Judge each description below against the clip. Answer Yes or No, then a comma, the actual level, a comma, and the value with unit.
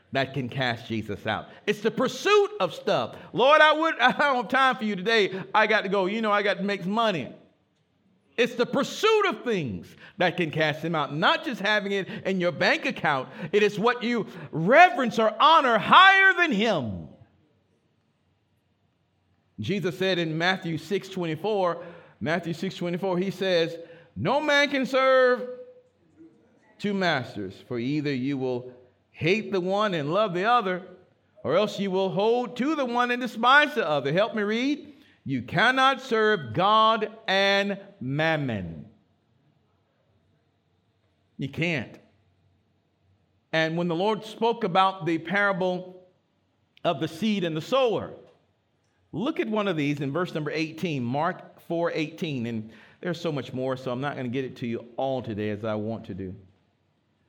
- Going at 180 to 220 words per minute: No, average, 165 wpm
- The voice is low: No, medium, 180 Hz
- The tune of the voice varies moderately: No, wide, 8.7 semitones